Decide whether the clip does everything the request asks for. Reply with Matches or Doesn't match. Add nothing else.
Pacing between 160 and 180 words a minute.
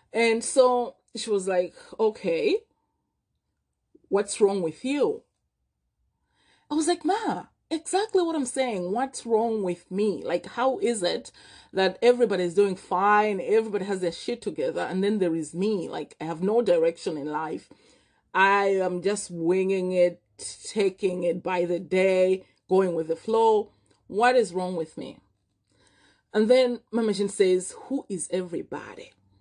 Doesn't match